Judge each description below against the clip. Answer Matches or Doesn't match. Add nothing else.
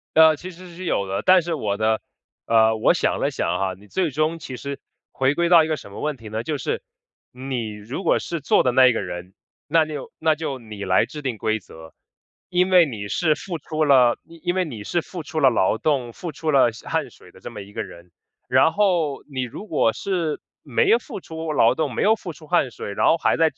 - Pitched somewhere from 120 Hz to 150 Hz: Matches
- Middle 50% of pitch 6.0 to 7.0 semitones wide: Matches